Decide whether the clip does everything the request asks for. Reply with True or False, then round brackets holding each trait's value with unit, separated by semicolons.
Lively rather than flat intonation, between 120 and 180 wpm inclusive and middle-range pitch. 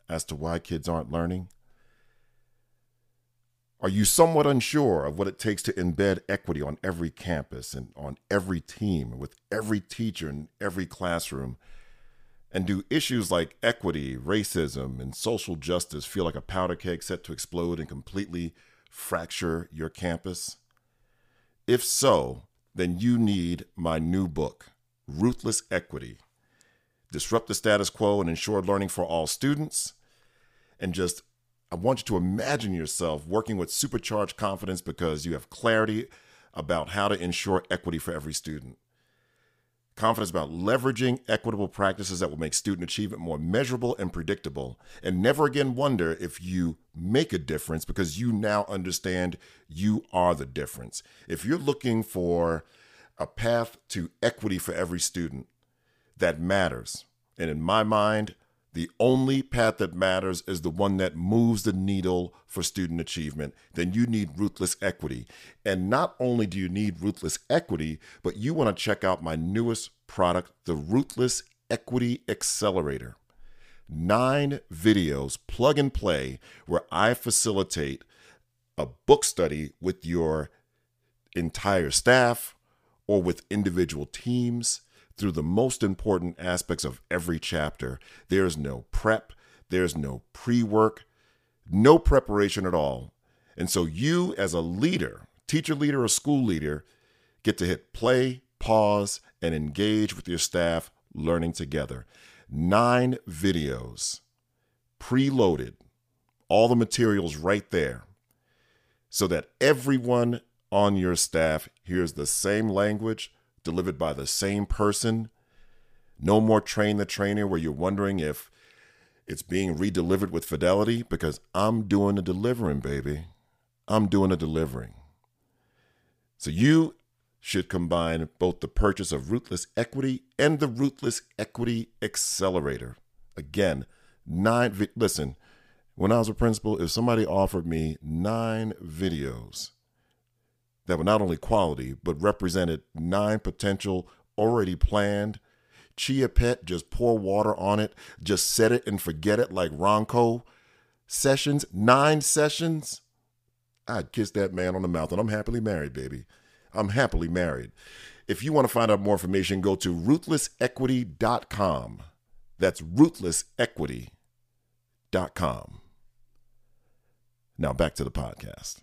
False (5.7 semitones; 135 wpm; 100 Hz)